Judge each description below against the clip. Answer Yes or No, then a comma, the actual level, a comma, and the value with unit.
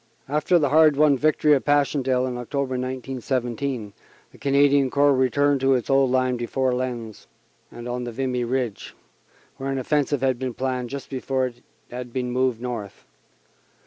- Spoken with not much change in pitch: Yes, narrow, 2.1 semitones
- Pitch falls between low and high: No, low, 130 Hz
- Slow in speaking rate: No, average, 160 wpm